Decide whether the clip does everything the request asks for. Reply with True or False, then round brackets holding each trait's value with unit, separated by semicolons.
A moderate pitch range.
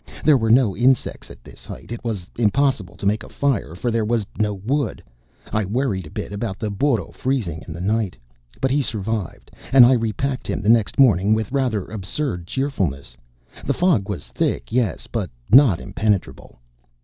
True (4.6 semitones)